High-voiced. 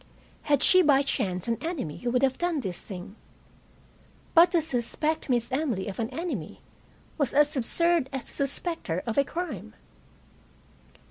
Yes: very high, 270 Hz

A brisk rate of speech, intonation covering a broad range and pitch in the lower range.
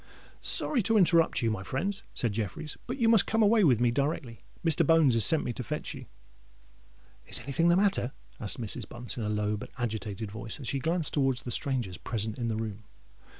Yes: fast, 210 wpm; wide, 6.8 semitones; low, 125 Hz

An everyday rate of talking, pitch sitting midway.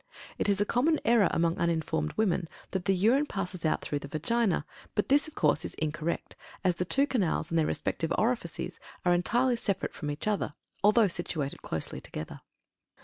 Yes: average, 185 wpm; medium, 180 Hz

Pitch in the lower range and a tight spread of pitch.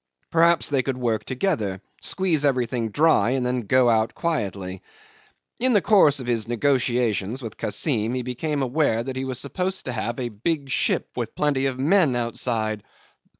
No: low, 125 Hz; average, 4.2 semitones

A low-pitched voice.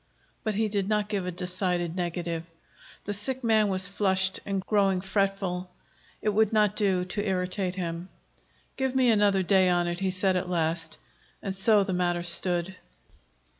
No: high, 190 Hz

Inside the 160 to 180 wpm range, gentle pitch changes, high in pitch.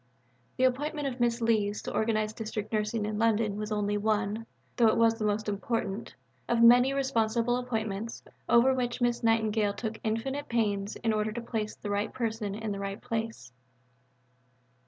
Yes: average, 170 wpm; narrow, 2.0 semitones; high, 225 Hz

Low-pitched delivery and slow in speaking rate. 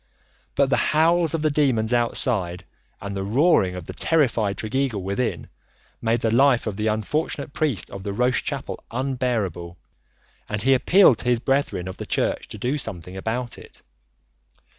No: low, 120 Hz; average, 165 wpm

